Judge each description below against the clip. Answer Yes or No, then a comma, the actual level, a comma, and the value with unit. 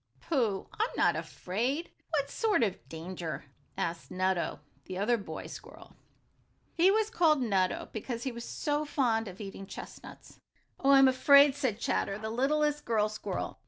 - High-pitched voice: Yes, high, 235 Hz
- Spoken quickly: No, average, 155 wpm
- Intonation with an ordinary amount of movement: No, wide, 6.5 semitones